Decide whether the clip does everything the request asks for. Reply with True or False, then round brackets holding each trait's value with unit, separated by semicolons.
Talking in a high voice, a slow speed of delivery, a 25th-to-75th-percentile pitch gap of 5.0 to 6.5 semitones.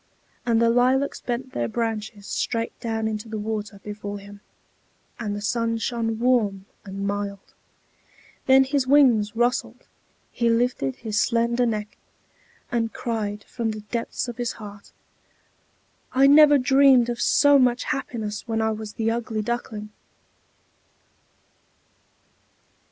False (230 Hz; 130 wpm; 2.7 semitones)